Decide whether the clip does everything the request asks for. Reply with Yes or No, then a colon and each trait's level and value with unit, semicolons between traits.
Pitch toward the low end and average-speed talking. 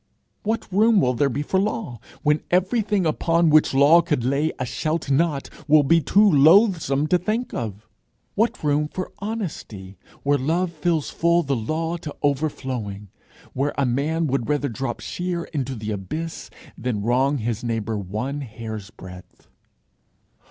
No: medium, 145 Hz; average, 155 wpm